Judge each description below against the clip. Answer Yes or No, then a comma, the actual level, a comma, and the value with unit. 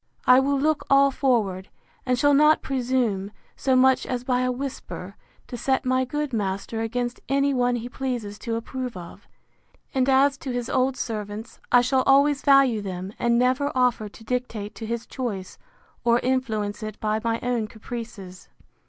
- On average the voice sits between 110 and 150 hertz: No, high, 245 Hz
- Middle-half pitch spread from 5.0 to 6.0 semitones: No, average, 3.2 semitones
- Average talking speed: Yes, average, 170 wpm